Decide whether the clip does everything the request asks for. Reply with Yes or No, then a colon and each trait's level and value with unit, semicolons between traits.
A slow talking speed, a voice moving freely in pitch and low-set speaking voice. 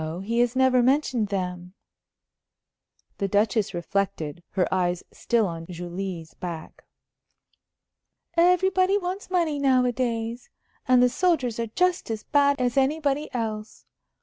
No: slow, 120 wpm; wide, 6.4 semitones; high, 235 Hz